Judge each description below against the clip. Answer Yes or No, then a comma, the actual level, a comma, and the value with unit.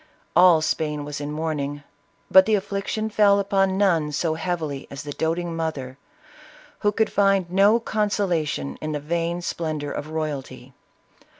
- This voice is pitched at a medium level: Yes, medium, 165 Hz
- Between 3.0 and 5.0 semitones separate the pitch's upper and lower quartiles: Yes, average, 4.7 semitones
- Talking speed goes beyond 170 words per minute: No, average, 155 wpm